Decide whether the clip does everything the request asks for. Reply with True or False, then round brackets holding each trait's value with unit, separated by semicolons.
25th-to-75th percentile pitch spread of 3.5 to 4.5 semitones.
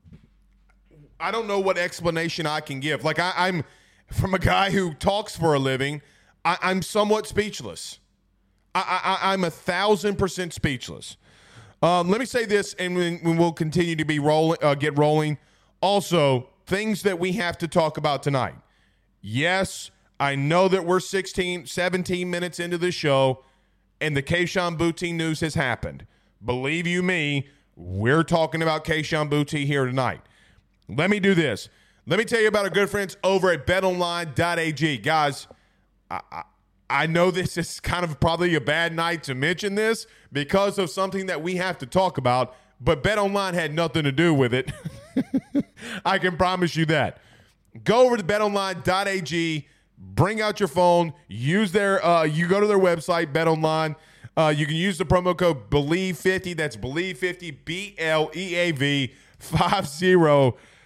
True (4.0 semitones)